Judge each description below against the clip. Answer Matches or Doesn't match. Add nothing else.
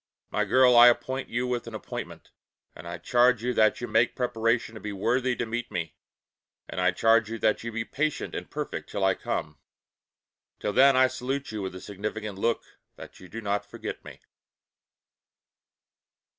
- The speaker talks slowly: Doesn't match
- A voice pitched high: Doesn't match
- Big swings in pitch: Doesn't match